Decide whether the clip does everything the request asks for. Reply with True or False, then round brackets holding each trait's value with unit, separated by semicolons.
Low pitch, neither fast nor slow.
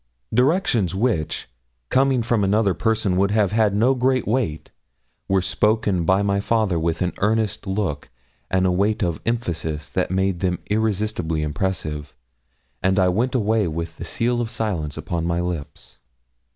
True (100 Hz; 155 wpm)